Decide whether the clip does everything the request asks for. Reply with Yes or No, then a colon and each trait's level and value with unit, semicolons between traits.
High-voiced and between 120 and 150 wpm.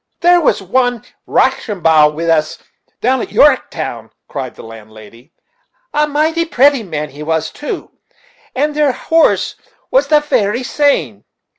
Yes: high, 235 Hz; slow, 135 wpm